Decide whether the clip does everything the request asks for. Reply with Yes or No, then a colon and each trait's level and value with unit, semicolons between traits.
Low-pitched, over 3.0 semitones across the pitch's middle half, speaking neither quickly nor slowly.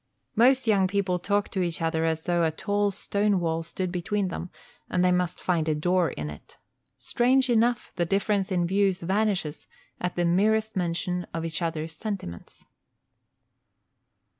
No: medium, 180 Hz; average, 3.4 semitones; average, 165 wpm